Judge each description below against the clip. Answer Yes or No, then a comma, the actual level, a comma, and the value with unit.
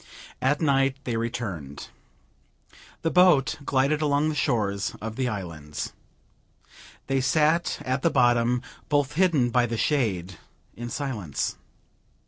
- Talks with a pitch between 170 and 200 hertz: No, low, 130 Hz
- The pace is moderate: No, slow, 120 wpm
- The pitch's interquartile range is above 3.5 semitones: Yes, average, 4.5 semitones